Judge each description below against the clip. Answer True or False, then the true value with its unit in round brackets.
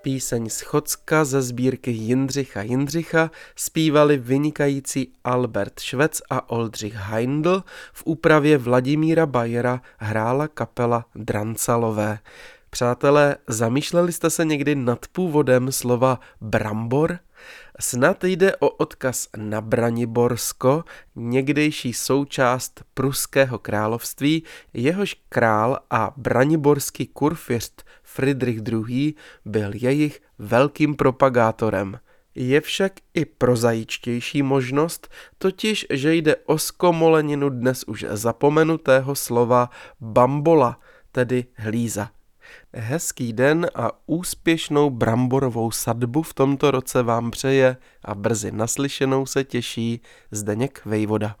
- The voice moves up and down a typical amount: True (4.2 semitones)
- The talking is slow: True (100 wpm)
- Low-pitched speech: True (130 Hz)